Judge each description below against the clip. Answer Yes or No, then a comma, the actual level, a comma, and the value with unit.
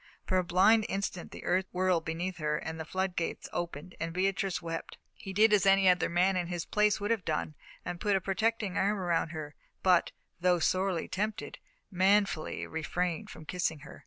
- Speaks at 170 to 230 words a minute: Yes, average, 190 wpm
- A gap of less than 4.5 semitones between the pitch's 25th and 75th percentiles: Yes, narrow, 2.5 semitones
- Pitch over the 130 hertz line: Yes, medium, 185 Hz